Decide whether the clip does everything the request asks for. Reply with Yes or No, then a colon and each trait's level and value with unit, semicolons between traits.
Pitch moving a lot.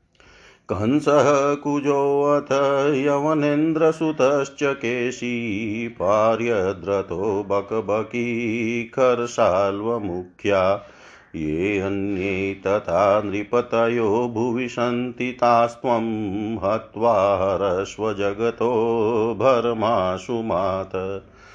No: average, 4.0 semitones